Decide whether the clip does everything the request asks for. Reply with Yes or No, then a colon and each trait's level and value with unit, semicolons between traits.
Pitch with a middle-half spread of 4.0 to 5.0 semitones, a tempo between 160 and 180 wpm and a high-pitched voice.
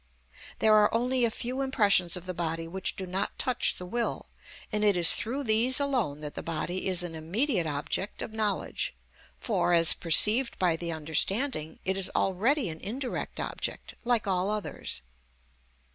No: wide, 5.5 semitones; average, 170 wpm; high, 195 Hz